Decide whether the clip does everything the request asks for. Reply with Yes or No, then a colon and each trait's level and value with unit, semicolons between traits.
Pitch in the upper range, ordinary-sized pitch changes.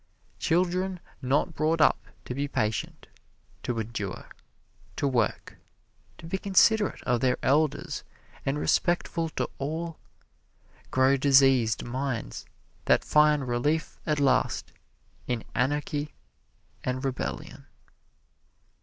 No: medium, 140 Hz; average, 4.0 semitones